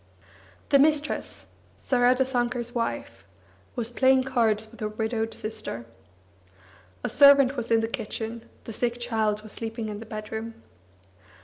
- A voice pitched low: No, high, 230 Hz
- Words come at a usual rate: No, slow, 130 wpm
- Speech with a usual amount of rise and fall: No, narrow, 2.2 semitones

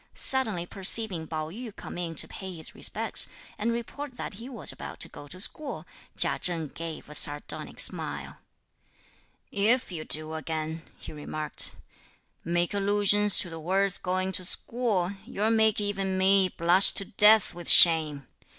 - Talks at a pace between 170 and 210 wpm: No, average, 160 wpm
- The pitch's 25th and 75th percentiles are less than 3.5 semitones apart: No, average, 4.1 semitones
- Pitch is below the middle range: No, medium, 185 Hz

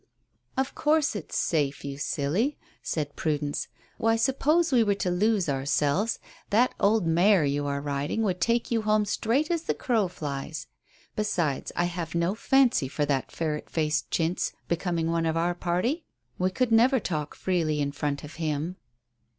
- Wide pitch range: Yes, wide, 6.9 semitones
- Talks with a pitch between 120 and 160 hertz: No, medium, 175 Hz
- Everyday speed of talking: Yes, average, 165 wpm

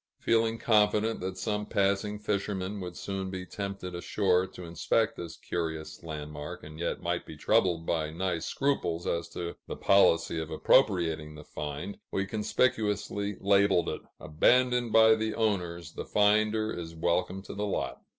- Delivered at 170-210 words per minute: No, average, 155 wpm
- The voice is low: Yes, very low, 95 Hz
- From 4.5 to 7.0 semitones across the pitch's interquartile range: No, average, 3.8 semitones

